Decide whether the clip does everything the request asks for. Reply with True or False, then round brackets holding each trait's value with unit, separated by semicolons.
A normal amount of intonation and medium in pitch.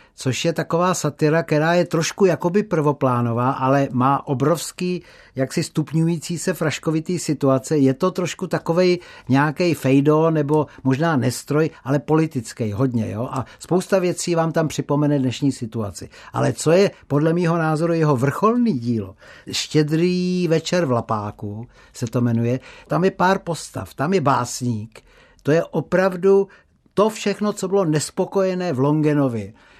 True (4.8 semitones; 155 Hz)